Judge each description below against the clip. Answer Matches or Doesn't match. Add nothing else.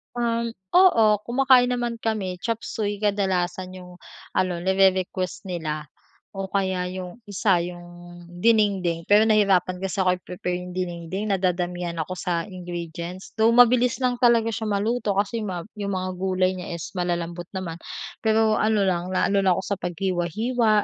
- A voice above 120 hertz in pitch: Matches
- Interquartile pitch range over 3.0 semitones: Matches